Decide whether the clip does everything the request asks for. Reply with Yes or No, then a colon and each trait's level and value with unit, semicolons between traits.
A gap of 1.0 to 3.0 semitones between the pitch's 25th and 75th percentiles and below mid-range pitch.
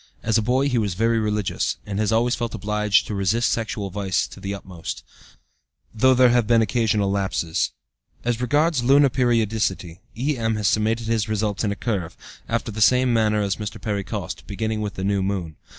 Yes: average, 2.7 semitones; low, 110 Hz